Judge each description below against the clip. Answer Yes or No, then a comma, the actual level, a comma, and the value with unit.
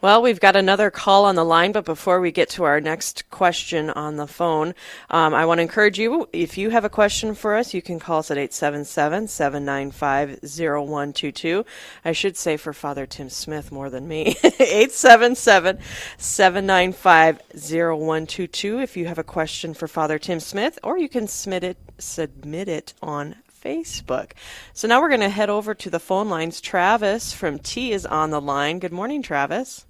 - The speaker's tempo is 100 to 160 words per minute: No, average, 180 wpm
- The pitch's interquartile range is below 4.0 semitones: No, average, 5.0 semitones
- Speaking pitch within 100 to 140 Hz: No, medium, 170 Hz